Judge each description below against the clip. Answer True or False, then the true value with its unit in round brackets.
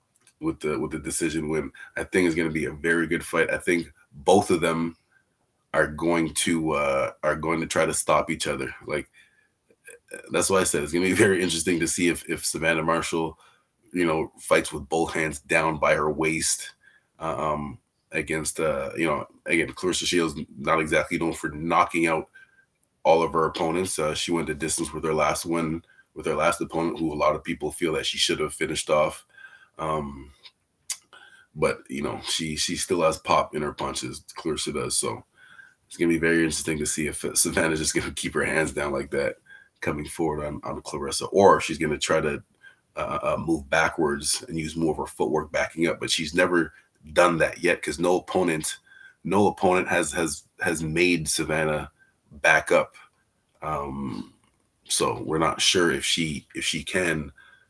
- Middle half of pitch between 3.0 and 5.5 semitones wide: False (2.6 semitones)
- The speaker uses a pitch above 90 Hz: False (80 Hz)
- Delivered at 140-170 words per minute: False (195 wpm)